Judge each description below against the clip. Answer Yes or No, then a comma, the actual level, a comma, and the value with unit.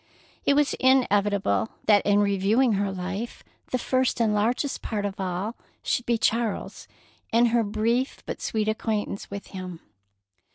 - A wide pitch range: No, average, 3.0 semitones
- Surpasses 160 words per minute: No, average, 150 wpm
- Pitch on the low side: No, high, 215 Hz